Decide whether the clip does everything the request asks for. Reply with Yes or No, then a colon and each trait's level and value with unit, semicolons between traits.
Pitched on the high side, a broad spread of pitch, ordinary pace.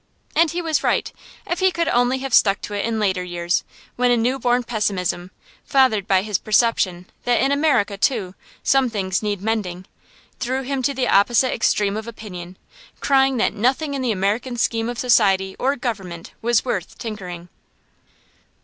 No: high, 225 Hz; average, 4.8 semitones; average, 175 wpm